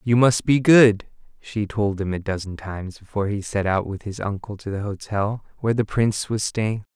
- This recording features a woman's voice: No, male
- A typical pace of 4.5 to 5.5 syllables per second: Yes, 5.3 syllables/s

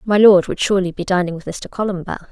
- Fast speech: Yes, fast, 235 wpm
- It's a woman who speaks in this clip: Yes, female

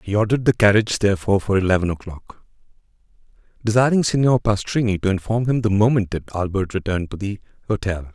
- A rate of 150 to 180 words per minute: Yes, average, 160 wpm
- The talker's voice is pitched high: No, low, 105 Hz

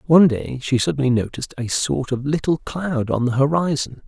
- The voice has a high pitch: No, low, 135 Hz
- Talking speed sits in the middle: Yes, average, 190 wpm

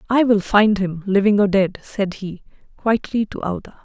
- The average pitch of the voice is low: No, high, 200 Hz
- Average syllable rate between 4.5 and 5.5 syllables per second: Yes, 5.0 syllables/s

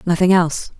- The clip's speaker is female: Yes, female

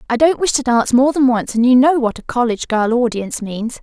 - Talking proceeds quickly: Yes, fast, 265 wpm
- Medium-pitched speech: No, high, 245 Hz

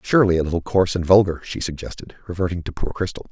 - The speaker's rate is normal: No, fast, 215 wpm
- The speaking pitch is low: Yes, very low, 90 Hz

